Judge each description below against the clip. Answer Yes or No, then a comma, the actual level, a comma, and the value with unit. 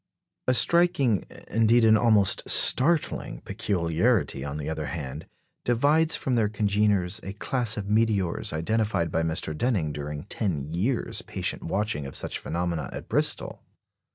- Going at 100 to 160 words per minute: Yes, average, 140 wpm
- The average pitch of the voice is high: No, low, 100 Hz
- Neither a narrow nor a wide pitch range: No, wide, 5.9 semitones